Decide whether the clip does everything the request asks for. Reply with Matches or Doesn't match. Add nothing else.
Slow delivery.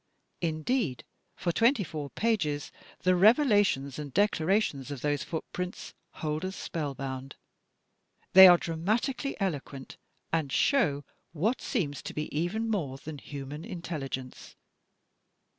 Matches